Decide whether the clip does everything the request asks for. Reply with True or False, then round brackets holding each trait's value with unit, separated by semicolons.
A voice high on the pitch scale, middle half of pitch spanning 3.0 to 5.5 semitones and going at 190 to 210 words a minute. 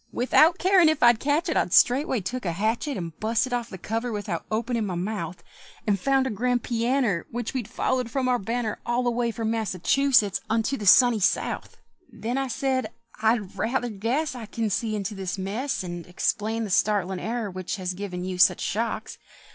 True (225 Hz; 3.9 semitones; 195 wpm)